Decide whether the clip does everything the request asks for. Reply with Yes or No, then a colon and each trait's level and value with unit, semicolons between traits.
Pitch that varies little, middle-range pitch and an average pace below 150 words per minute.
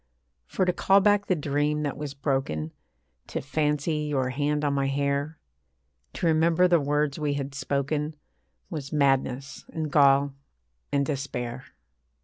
Yes: narrow, 1.8 semitones; medium, 145 Hz; average, 140 wpm